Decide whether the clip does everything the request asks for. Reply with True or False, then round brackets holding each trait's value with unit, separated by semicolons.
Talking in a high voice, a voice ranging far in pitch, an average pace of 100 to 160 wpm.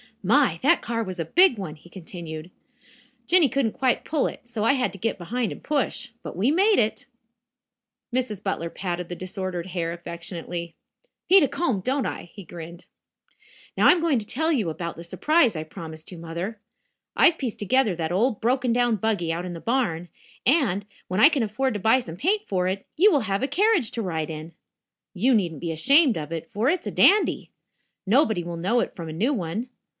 False (205 Hz; 7.2 semitones; 205 wpm)